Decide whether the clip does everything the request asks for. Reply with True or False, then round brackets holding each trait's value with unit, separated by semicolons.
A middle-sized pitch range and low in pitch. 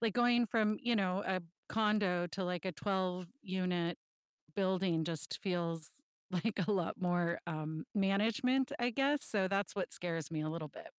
False (3.7 semitones; 185 Hz)